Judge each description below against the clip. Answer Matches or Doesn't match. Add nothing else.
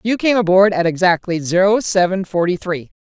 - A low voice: Doesn't match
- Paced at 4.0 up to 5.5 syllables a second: Matches